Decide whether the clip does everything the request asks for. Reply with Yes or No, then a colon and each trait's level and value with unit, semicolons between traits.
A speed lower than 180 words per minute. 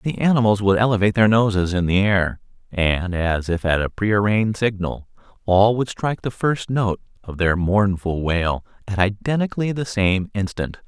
Yes: average, 170 wpm